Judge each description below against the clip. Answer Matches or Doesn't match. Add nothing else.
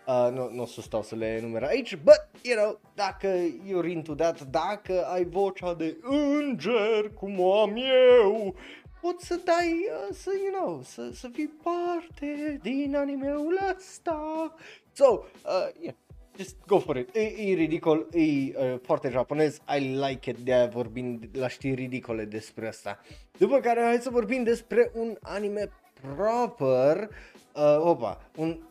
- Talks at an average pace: Matches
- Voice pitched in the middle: Doesn't match